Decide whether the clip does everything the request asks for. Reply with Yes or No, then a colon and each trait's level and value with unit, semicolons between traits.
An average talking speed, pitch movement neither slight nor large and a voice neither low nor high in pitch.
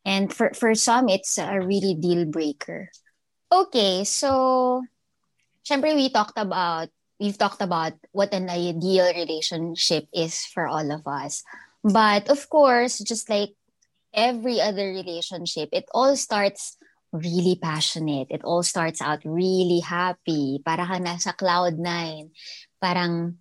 Yes: average, 130 wpm; average, 4.1 semitones; medium, 180 Hz